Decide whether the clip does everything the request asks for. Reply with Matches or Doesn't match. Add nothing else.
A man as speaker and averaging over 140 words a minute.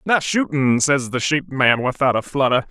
Matches